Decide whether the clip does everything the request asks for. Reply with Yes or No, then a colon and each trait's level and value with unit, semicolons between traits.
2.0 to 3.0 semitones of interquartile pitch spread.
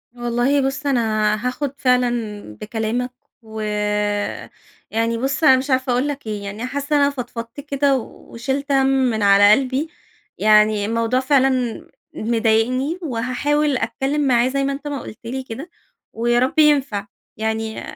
No: average, 3.5 semitones